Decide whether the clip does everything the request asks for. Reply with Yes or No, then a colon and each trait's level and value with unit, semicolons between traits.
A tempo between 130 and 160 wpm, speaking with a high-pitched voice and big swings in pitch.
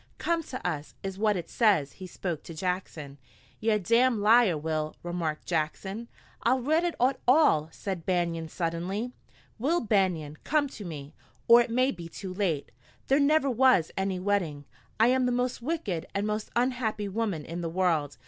No: average, 175 wpm; high, 195 Hz; wide, 6.4 semitones